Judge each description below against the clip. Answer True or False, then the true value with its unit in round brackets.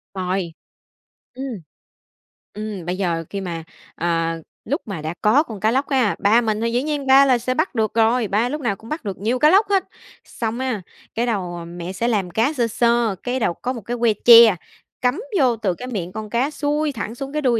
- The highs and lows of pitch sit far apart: False (4.6 semitones)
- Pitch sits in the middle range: False (230 Hz)